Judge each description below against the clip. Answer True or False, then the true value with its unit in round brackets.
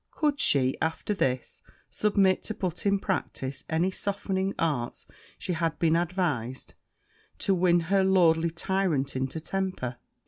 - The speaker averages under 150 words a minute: True (135 wpm)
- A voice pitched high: False (175 Hz)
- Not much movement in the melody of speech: False (4.1 semitones)